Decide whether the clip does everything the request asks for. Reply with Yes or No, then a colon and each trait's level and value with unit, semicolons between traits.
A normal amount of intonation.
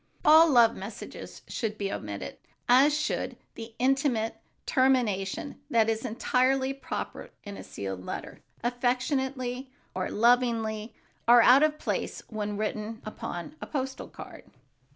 Yes: average, 3.6 semitones